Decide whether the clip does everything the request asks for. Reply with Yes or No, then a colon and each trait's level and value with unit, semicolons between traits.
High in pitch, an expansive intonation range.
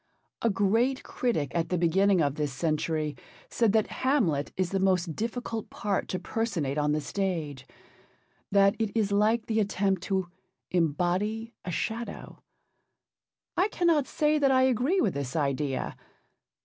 Yes: high, 195 Hz; wide, 6.0 semitones